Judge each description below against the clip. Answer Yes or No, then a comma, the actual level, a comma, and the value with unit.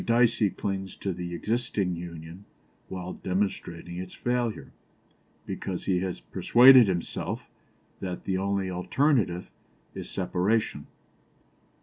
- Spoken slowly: Yes, slow, 105 wpm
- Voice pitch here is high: No, very low, 95 Hz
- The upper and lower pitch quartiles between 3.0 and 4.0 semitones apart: Yes, average, 3.4 semitones